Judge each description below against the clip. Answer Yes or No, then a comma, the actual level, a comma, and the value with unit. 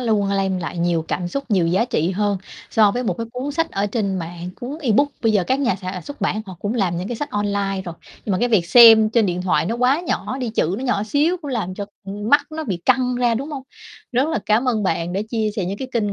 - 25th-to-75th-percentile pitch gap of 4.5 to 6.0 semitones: Yes, average, 4.8 semitones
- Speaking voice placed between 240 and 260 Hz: No, high, 215 Hz